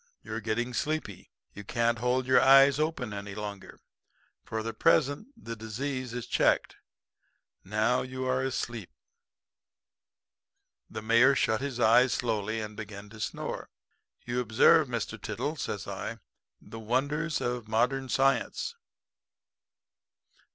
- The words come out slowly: Yes, slow, 125 wpm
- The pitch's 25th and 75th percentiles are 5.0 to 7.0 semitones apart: No, average, 3.1 semitones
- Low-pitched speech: Yes, low, 120 Hz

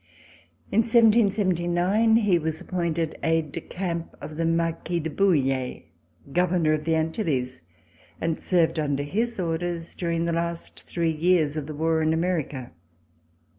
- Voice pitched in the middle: Yes, medium, 165 Hz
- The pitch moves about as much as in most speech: No, narrow, 2.3 semitones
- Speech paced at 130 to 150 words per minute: Yes, average, 140 wpm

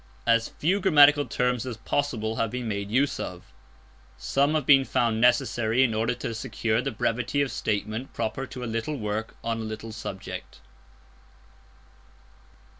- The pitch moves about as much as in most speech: Yes, average, 3.4 semitones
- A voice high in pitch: No, low, 115 Hz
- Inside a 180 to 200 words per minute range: No, average, 155 wpm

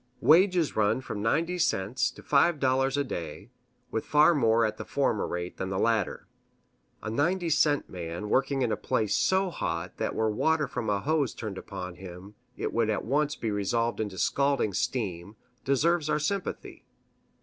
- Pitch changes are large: Yes, wide, 6.4 semitones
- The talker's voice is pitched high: No, low, 115 Hz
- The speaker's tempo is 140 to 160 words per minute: No, average, 175 wpm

